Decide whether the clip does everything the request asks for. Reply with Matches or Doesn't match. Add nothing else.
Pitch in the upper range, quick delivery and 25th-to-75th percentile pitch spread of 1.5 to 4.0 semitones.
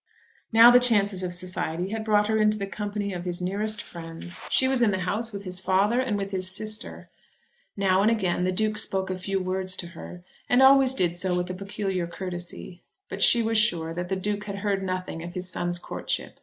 Matches